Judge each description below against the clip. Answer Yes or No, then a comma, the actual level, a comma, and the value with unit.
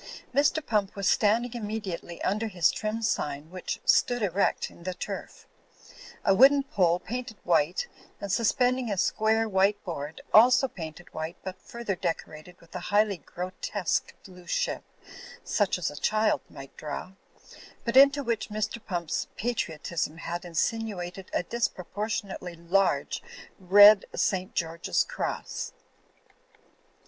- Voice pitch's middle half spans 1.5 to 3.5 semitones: No, average, 4.3 semitones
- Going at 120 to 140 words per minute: Yes, slow, 135 wpm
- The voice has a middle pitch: No, high, 195 Hz